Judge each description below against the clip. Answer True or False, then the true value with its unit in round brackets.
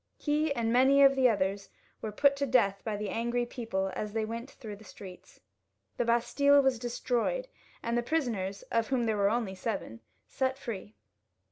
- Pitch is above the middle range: True (235 Hz)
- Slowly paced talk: False (180 wpm)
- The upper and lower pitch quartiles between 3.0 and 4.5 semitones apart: True (4.1 semitones)